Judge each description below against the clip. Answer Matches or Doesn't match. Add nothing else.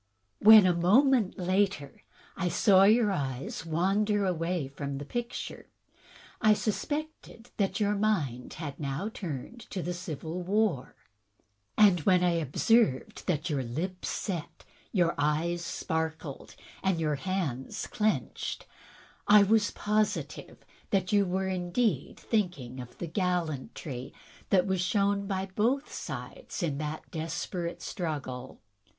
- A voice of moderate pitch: Matches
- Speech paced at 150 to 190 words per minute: Doesn't match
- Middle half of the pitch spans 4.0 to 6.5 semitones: Matches